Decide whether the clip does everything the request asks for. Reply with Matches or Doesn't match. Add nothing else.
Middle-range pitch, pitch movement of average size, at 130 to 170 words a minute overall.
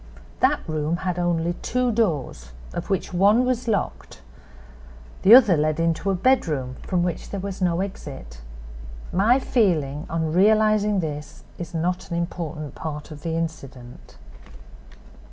Matches